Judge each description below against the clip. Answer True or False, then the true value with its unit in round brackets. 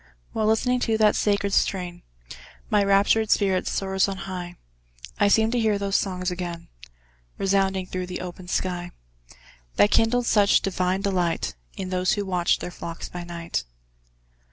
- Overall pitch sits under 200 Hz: True (190 Hz)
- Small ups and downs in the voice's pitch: True (2.2 semitones)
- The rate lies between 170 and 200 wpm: False (155 wpm)